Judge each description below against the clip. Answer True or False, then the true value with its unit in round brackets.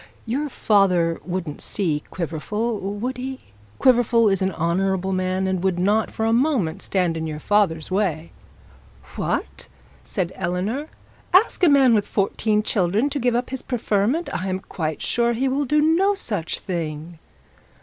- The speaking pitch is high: True (200 Hz)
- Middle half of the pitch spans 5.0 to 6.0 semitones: True (5.5 semitones)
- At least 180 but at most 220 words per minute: False (160 wpm)